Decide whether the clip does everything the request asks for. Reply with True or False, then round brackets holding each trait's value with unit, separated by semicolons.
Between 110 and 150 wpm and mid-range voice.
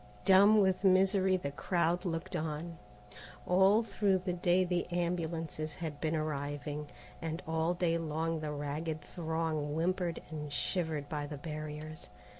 True (140 wpm; 165 Hz)